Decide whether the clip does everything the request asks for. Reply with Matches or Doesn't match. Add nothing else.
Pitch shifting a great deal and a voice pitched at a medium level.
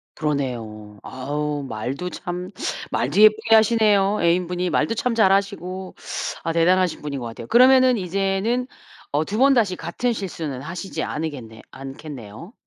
Matches